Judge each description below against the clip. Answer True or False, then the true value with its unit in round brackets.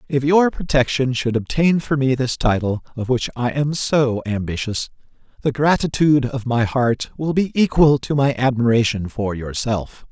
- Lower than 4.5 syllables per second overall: False (4.6 syllables/s)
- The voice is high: False (130 Hz)